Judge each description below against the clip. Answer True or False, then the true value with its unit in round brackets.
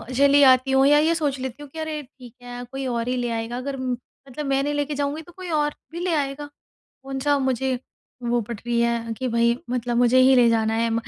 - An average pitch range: True (3.3 semitones)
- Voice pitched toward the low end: False (260 Hz)